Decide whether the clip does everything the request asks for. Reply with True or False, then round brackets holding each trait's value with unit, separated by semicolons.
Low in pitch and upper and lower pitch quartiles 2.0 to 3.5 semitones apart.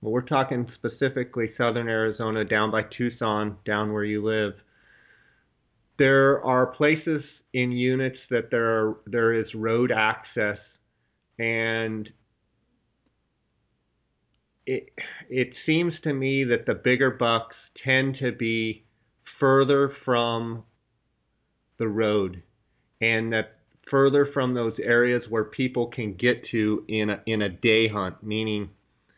True (115 Hz; 2.7 semitones)